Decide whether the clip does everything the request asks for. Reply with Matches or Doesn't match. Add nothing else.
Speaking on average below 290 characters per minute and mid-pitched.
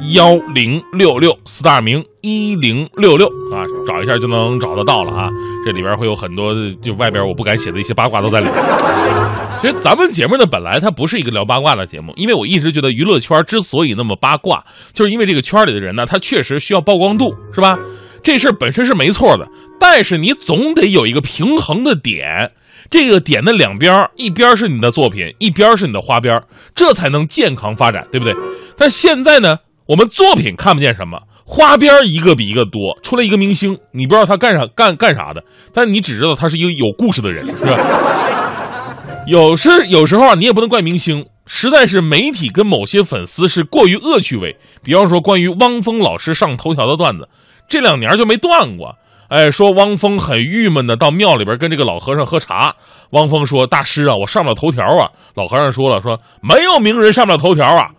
Doesn't match